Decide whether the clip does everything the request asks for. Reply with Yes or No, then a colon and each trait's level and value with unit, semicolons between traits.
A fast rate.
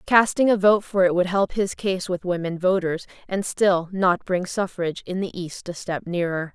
Yes: fast, 210 wpm